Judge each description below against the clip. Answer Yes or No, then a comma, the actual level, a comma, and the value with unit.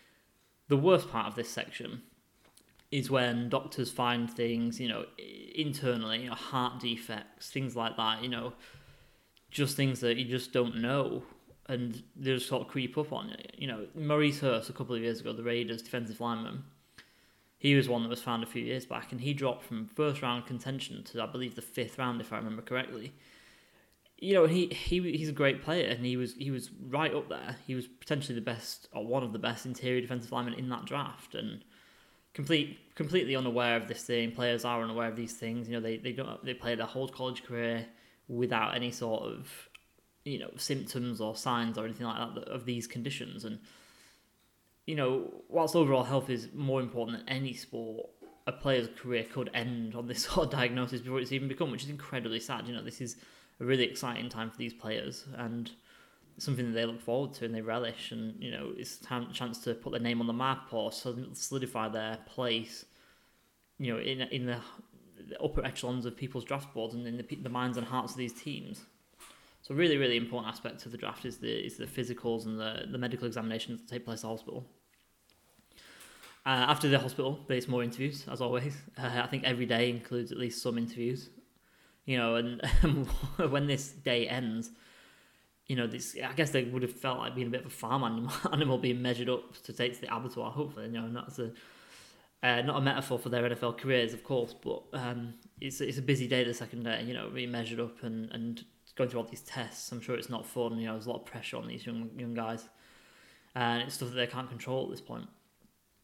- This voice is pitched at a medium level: No, low, 125 Hz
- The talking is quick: Yes, fast, 215 wpm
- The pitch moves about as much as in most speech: No, narrow, 1.9 semitones